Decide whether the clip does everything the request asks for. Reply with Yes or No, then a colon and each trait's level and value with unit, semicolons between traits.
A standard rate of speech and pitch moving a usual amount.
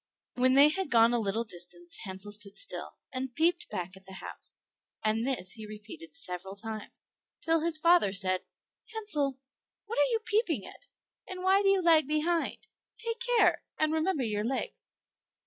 No: average, 170 wpm; wide, 8.8 semitones